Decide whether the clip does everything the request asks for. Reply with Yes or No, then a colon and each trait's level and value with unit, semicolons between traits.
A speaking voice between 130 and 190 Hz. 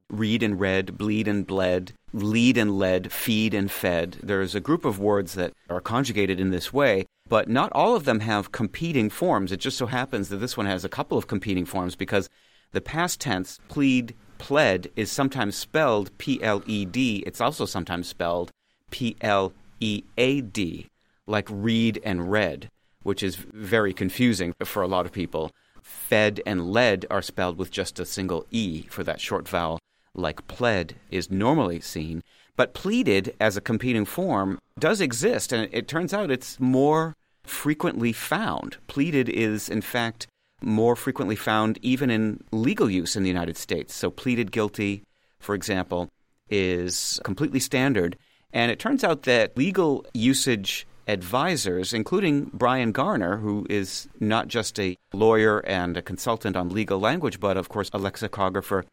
No: low, 105 Hz